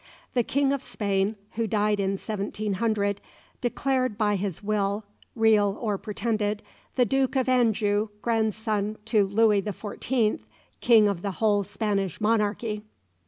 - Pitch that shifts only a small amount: Yes, narrow, 1.9 semitones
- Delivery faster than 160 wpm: No, slow, 135 wpm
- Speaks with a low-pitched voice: No, high, 210 Hz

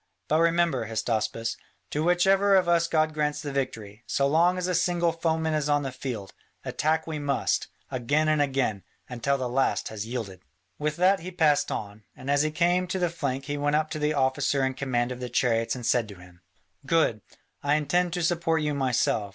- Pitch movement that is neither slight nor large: Yes, average, 4.6 semitones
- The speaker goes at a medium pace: No, fast, 210 wpm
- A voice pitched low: No, medium, 145 Hz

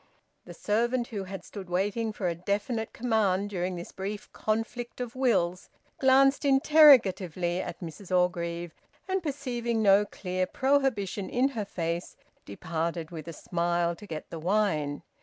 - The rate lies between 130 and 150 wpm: Yes, average, 145 wpm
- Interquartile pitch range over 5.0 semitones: Yes, wide, 5.4 semitones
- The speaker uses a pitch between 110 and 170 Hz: No, high, 200 Hz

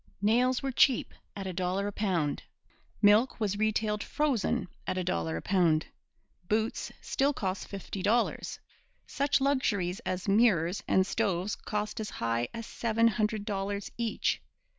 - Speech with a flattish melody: No, average, 3.5 semitones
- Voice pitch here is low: No, high, 205 Hz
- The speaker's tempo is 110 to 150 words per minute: Yes, average, 145 wpm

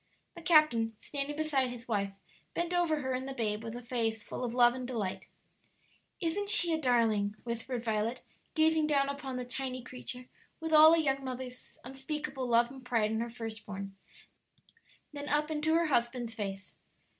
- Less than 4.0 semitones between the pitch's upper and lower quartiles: No, average, 4.5 semitones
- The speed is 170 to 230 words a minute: Yes, average, 180 wpm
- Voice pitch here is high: Yes, very high, 255 Hz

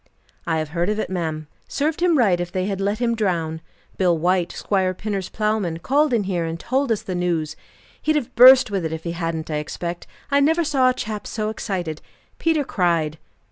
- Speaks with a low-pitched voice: No, high, 190 Hz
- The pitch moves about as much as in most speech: No, wide, 5.7 semitones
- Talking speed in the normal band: No, fast, 210 wpm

